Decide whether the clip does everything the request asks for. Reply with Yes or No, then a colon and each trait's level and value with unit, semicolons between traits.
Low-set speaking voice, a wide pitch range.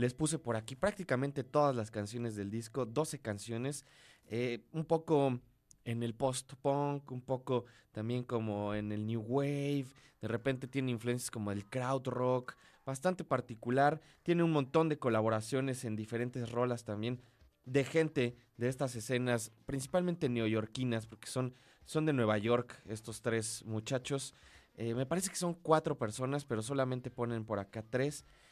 No: low, 125 Hz; average, 3.4 semitones